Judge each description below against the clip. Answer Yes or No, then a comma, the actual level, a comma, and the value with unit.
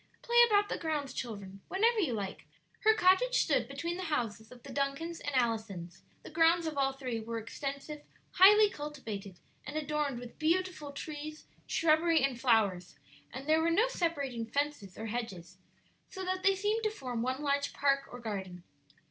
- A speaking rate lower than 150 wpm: No, average, 175 wpm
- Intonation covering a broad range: Yes, wide, 6.5 semitones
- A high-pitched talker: Yes, very high, 280 Hz